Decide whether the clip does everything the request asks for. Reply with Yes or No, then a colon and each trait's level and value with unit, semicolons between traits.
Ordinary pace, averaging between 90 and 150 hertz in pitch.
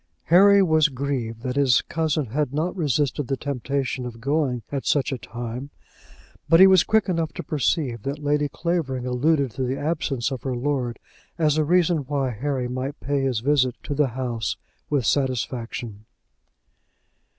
Yes: average, 165 wpm; medium, 140 Hz